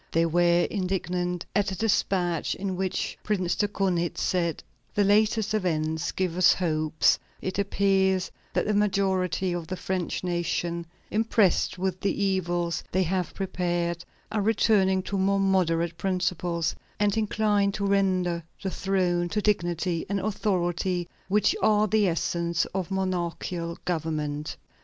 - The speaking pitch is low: No, medium, 185 Hz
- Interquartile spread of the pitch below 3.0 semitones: Yes, narrow, 2.4 semitones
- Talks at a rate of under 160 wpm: Yes, average, 140 wpm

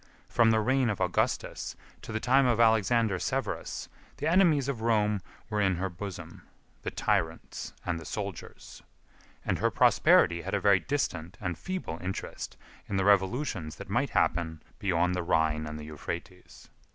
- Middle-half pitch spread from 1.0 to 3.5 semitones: No, average, 5.0 semitones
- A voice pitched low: Yes, low, 100 Hz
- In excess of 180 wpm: No, average, 160 wpm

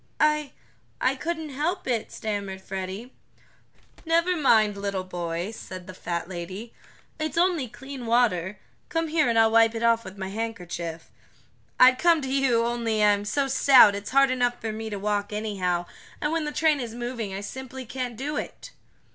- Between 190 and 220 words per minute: No, average, 175 wpm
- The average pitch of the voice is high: Yes, high, 230 Hz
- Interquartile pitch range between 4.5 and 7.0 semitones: Yes, average, 5.2 semitones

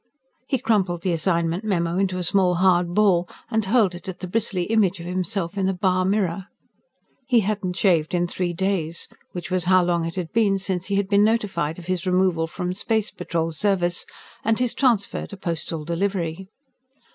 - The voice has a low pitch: No, medium, 185 Hz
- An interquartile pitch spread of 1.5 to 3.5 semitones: Yes, narrow, 2.6 semitones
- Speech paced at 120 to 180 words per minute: No, average, 190 wpm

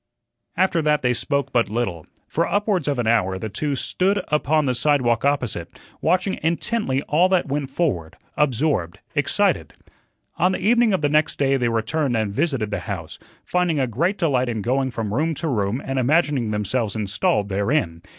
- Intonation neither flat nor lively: No, wide, 6.0 semitones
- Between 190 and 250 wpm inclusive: No, average, 180 wpm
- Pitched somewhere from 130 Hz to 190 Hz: Yes, low, 135 Hz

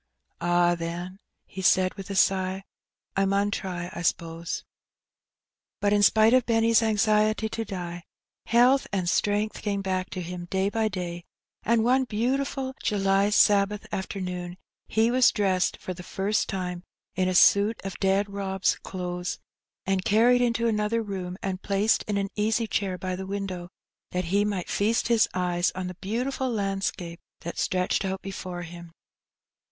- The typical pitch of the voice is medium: No, high, 195 Hz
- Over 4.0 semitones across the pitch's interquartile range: No, average, 2.9 semitones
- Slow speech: No, average, 165 wpm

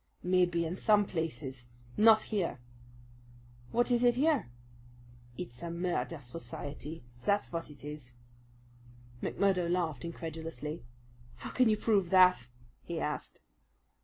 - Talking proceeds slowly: Yes, slow, 120 wpm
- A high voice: No, medium, 170 Hz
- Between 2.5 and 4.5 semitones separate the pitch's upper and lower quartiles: No, average, 4.9 semitones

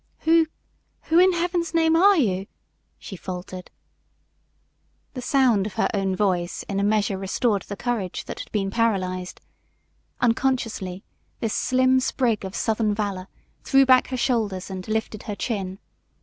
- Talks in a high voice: Yes, high, 215 Hz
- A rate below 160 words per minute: Yes, average, 150 wpm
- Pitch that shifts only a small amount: No, average, 5.0 semitones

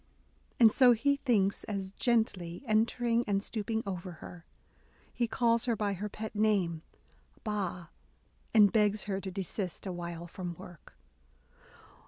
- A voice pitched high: Yes, high, 205 Hz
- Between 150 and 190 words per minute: No, average, 140 wpm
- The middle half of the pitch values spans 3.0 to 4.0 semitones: Yes, average, 3.6 semitones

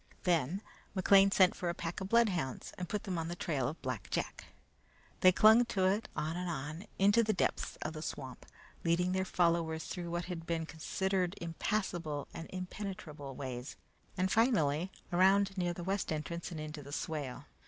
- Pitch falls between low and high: Yes, medium, 175 Hz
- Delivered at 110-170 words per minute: No, average, 180 wpm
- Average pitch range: Yes, average, 3.5 semitones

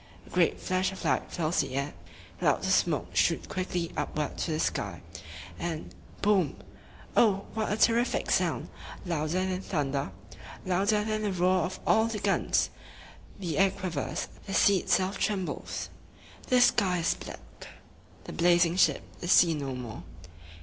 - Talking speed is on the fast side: No, average, 160 wpm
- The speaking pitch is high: No, medium, 180 Hz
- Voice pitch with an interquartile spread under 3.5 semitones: No, average, 4.0 semitones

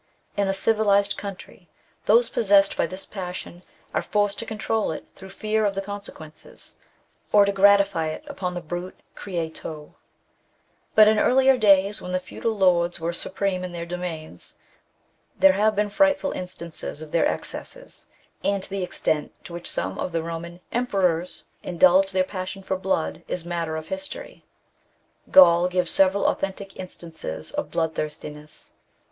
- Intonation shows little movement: No, average, 3.0 semitones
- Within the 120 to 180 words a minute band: Yes, average, 155 wpm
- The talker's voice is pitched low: No, medium, 185 Hz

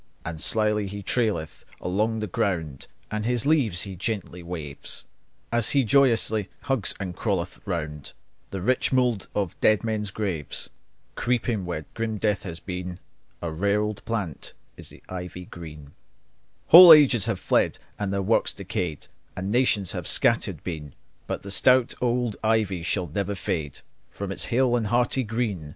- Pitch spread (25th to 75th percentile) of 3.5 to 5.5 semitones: Yes, average, 4.3 semitones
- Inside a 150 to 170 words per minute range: Yes, average, 160 wpm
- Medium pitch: No, low, 100 Hz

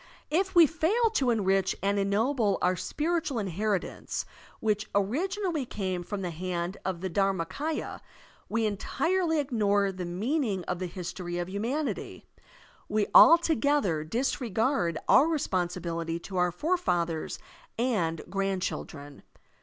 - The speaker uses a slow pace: Yes, slow, 120 wpm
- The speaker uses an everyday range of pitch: No, wide, 7.9 semitones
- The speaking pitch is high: Yes, high, 200 Hz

